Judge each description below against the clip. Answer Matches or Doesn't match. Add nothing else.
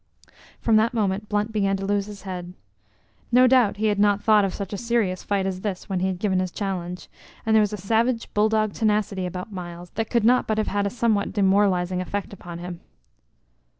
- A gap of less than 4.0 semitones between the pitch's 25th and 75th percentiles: Matches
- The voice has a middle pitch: Doesn't match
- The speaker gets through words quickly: Matches